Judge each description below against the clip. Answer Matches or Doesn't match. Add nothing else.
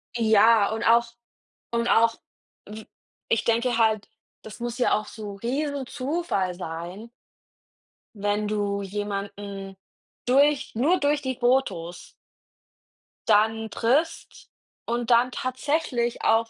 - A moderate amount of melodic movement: Matches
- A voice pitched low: Doesn't match